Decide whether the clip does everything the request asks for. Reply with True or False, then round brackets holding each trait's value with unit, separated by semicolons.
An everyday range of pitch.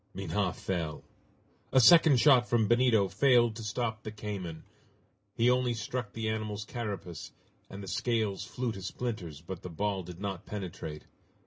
True (3.9 semitones)